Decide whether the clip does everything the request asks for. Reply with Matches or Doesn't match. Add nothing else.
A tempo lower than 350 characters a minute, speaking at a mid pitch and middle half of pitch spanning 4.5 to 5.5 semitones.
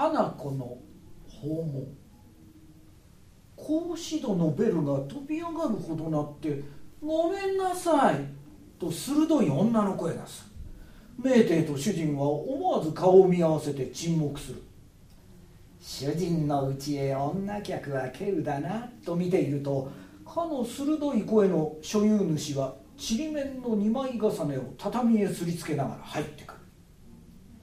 Doesn't match